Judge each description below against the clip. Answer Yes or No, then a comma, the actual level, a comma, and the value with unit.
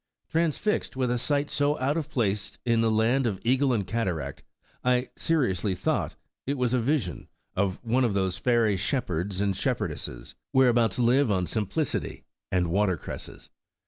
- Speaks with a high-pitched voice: No, low, 115 Hz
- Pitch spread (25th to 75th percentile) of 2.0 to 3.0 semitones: No, average, 5.3 semitones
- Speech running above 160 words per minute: Yes, average, 170 wpm